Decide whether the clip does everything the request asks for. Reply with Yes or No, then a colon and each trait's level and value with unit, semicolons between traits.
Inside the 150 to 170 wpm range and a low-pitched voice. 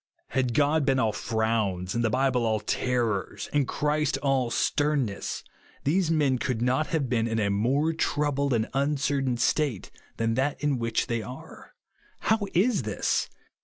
Yes: average, 160 wpm; low, 130 Hz